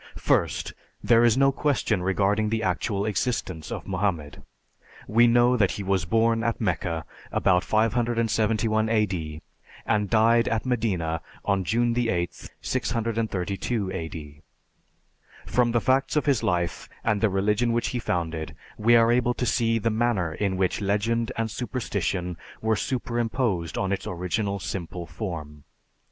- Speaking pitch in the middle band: No, low, 110 Hz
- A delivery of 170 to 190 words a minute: No, average, 140 wpm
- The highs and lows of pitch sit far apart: No, average, 4.1 semitones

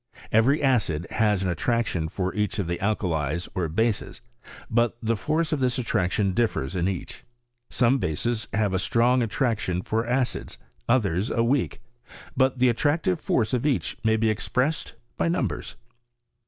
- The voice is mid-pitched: No, low, 110 Hz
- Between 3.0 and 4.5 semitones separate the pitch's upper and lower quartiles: No, average, 5.1 semitones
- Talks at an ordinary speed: Yes, average, 160 wpm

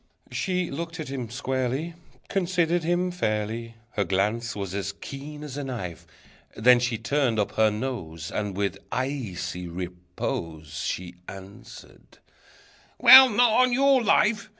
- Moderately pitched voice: No, low, 125 Hz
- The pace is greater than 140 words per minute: No, slow, 135 wpm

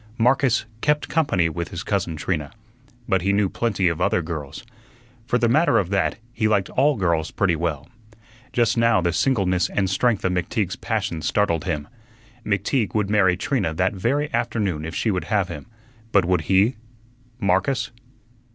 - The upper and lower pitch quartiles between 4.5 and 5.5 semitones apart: Yes, average, 5.0 semitones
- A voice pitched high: No, very low, 95 Hz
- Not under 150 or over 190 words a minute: Yes, average, 170 wpm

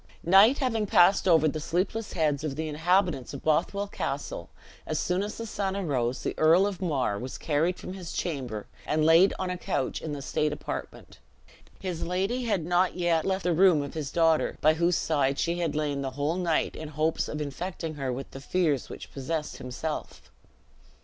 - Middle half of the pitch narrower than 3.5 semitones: No, average, 3.9 semitones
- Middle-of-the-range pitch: Yes, medium, 165 Hz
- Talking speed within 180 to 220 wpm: Yes, average, 195 wpm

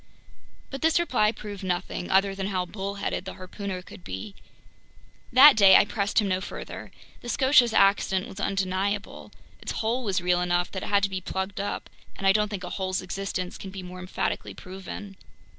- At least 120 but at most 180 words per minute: No, average, 190 wpm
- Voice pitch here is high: Yes, high, 195 Hz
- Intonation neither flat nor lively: No, narrow, 1.9 semitones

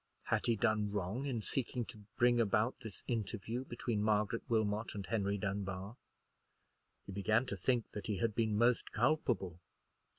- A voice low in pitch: Yes, low, 110 Hz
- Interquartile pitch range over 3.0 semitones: No, average, 2.7 semitones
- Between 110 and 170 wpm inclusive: Yes, average, 160 wpm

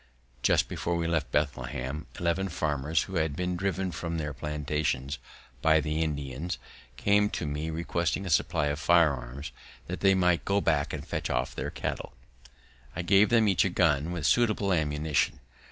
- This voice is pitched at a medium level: No, very low, 80 Hz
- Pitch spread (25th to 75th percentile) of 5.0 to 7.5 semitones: No, average, 3.4 semitones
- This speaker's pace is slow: No, average, 170 wpm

